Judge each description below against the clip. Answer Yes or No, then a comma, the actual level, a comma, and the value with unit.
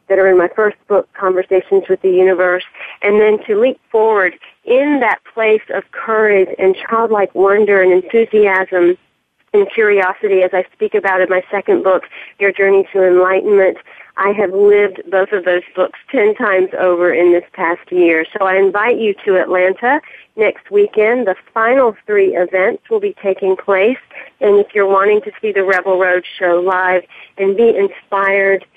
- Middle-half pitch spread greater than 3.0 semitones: No, narrow, 2.4 semitones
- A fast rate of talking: No, average, 175 wpm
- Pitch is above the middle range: Yes, high, 195 Hz